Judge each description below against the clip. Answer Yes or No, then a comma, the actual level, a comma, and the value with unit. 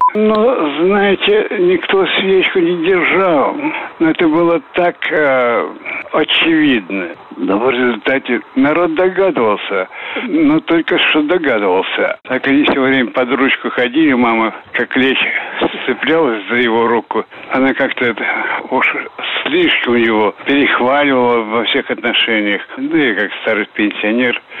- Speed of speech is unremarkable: Yes, average, 120 wpm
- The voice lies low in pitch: No, medium, 170 Hz